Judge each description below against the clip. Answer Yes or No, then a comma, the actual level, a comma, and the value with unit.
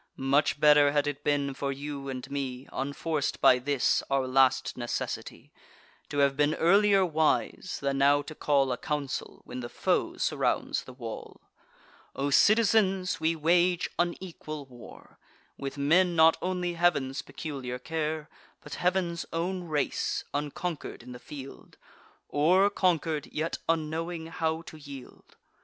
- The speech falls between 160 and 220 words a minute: No, average, 140 wpm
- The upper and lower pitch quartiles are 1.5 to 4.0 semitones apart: Yes, average, 3.5 semitones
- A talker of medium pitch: Yes, medium, 150 Hz